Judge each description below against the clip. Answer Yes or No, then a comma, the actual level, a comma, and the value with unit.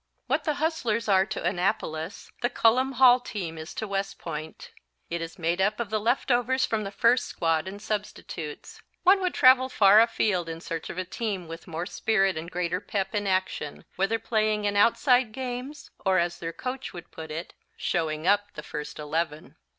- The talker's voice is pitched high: Yes, high, 200 Hz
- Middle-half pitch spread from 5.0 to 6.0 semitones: Yes, wide, 5.4 semitones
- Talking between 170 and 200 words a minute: Yes, average, 190 wpm